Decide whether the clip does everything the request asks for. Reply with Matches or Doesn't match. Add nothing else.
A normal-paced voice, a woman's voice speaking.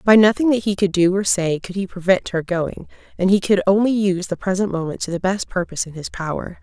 Doesn't match